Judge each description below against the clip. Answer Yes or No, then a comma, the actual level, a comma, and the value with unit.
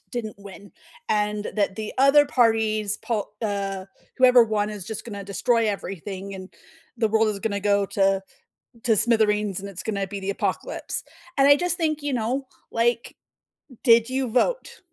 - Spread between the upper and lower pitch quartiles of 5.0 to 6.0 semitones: No, average, 3.1 semitones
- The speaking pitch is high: Yes, high, 215 Hz